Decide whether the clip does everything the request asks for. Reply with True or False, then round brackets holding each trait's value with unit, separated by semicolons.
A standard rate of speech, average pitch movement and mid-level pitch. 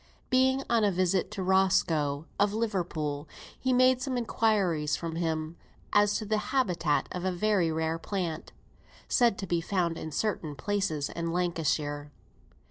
True (165 wpm; 4.7 semitones; 180 Hz)